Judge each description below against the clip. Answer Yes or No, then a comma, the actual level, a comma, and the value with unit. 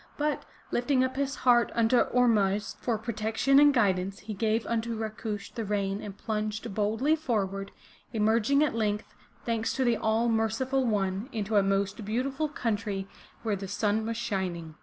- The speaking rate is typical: Yes, average, 165 wpm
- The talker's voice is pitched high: Yes, high, 220 Hz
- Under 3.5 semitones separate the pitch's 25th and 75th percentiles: Yes, average, 2.8 semitones